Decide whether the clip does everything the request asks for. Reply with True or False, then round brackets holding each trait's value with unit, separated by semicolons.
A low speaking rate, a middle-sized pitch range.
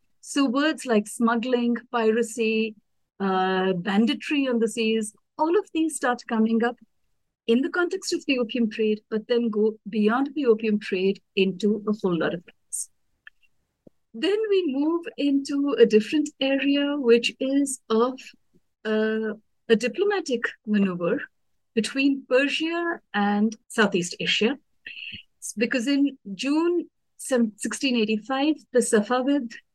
True (125 wpm; 4.4 semitones)